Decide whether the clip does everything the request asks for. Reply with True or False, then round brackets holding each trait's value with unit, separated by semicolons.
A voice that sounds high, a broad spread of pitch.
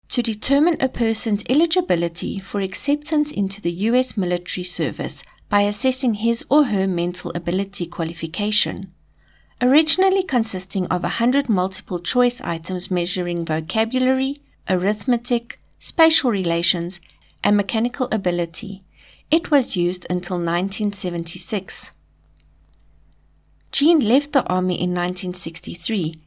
True (195 Hz; 5.8 semitones)